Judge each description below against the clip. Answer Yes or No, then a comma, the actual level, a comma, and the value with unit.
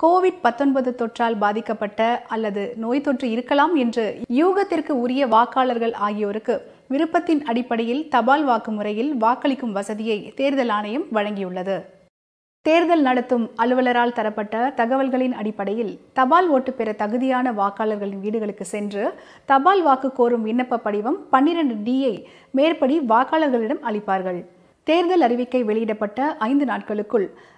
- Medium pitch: No, high, 240 Hz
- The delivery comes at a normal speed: Yes, average, 110 wpm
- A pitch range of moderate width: Yes, average, 4.0 semitones